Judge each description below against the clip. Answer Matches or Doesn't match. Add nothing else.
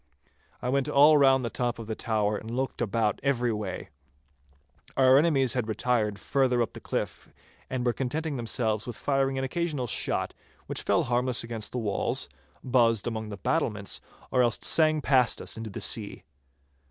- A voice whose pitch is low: Matches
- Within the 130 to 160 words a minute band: Doesn't match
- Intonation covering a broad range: Doesn't match